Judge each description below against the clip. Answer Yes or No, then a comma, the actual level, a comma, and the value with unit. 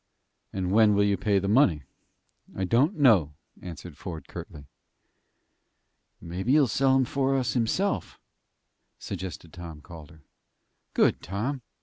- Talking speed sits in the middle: No, slow, 125 wpm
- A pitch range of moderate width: No, wide, 7.2 semitones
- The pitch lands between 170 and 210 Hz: No, low, 100 Hz